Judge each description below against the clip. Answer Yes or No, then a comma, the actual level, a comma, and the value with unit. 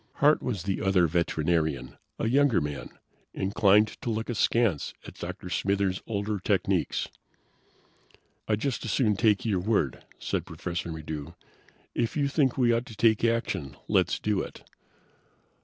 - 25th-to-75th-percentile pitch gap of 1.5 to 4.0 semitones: No, average, 5.2 semitones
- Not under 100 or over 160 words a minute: Yes, average, 145 wpm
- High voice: No, low, 105 Hz